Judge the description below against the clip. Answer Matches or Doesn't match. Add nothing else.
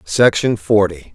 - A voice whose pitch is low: Matches